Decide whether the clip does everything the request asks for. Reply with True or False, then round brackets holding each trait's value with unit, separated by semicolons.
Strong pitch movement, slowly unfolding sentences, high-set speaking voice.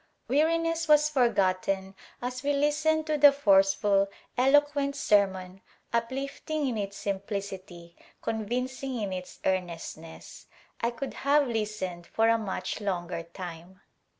True (6.6 semitones; 130 wpm; 220 Hz)